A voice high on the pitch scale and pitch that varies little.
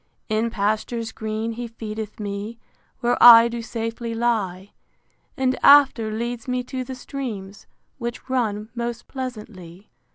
Yes: high, 230 Hz; narrow, 2.2 semitones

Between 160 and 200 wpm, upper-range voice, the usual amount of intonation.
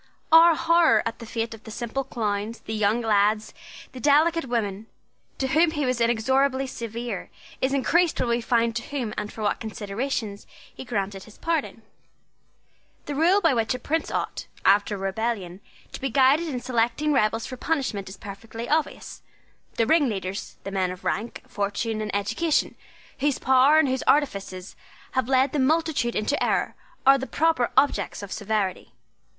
Yes: average, 170 wpm; high, 235 Hz; average, 4.7 semitones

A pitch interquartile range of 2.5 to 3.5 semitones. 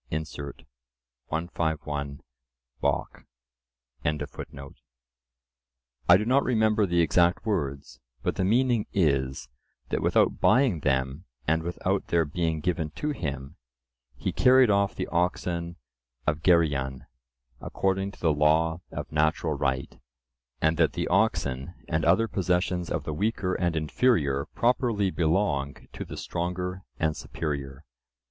No: average, 4.7 semitones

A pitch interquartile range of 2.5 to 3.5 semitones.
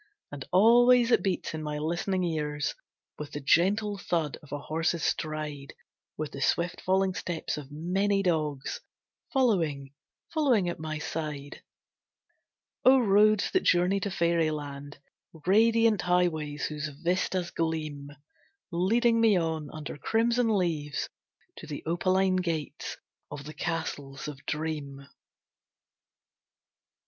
No: average, 4.5 semitones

